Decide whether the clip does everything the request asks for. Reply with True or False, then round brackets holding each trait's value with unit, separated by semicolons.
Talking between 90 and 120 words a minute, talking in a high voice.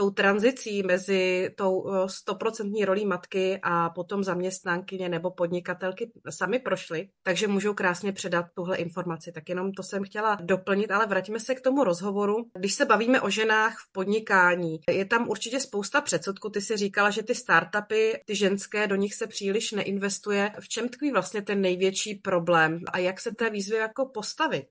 False (170 wpm; 200 Hz)